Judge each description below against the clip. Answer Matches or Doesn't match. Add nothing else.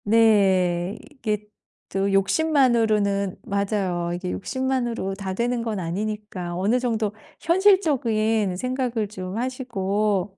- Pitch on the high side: Matches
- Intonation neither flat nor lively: Matches